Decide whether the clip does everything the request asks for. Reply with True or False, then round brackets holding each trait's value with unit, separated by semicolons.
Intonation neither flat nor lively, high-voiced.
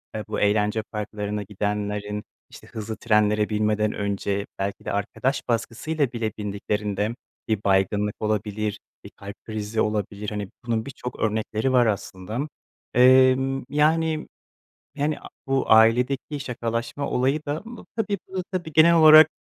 False (4.4 semitones; 110 Hz)